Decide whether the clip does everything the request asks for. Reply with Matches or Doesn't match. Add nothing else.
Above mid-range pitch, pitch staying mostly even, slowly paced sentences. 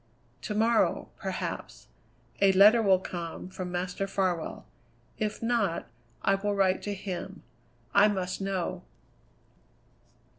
Matches